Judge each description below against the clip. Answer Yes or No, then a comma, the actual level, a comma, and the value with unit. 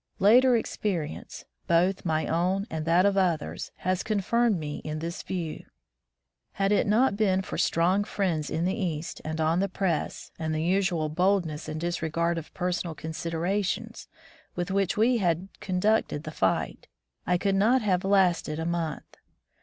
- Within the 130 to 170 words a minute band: Yes, average, 160 wpm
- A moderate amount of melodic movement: Yes, average, 3.4 semitones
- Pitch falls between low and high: Yes, medium, 180 Hz